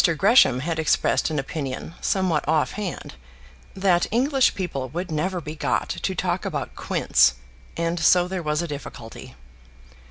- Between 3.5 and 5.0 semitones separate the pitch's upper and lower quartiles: Yes, average, 3.8 semitones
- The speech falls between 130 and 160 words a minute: Yes, average, 150 wpm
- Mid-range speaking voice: Yes, medium, 165 Hz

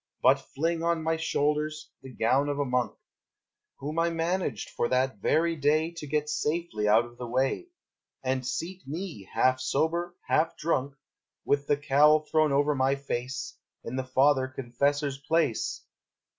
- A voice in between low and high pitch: Yes, medium, 145 Hz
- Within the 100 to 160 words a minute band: Yes, average, 155 wpm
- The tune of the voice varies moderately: Yes, average, 3.6 semitones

